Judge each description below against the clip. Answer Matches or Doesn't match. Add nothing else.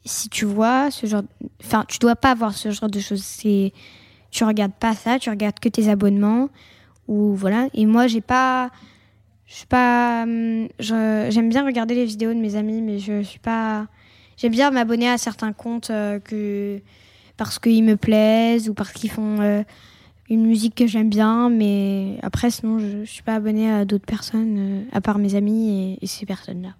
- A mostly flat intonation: Matches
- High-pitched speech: Matches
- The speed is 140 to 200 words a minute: Matches